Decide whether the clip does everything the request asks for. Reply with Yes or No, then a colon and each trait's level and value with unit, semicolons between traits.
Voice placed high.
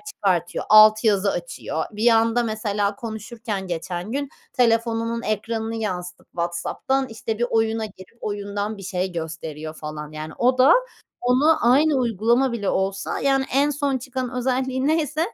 Yes: high, 225 Hz